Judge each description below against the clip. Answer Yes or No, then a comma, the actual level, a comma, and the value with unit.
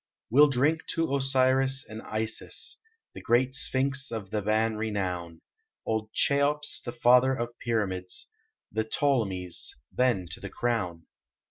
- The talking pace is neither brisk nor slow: No, slow, 130 wpm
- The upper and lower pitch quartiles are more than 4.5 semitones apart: No, average, 3.8 semitones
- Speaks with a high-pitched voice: No, low, 120 Hz